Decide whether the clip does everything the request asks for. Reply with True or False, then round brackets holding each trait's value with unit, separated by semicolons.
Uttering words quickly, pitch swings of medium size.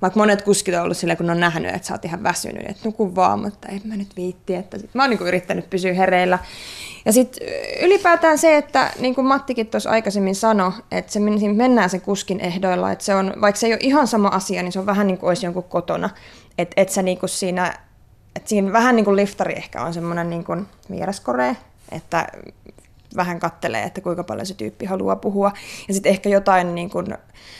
True (215 wpm; 3.1 semitones)